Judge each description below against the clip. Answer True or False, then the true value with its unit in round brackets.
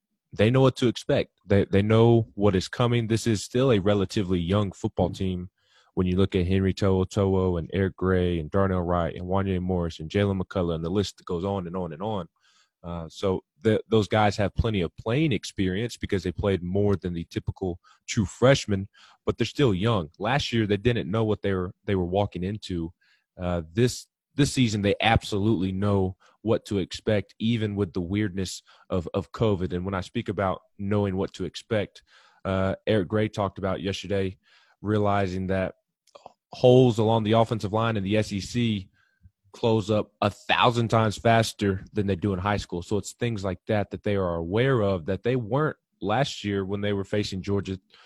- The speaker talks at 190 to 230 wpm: True (195 wpm)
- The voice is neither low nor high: False (100 Hz)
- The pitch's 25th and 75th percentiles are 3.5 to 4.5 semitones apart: False (2.8 semitones)